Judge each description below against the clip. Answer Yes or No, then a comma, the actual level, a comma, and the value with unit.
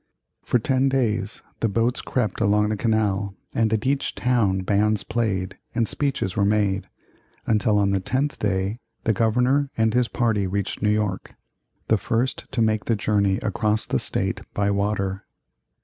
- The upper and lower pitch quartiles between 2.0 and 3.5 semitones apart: Yes, narrow, 2.6 semitones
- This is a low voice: Yes, low, 105 Hz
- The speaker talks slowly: No, average, 165 wpm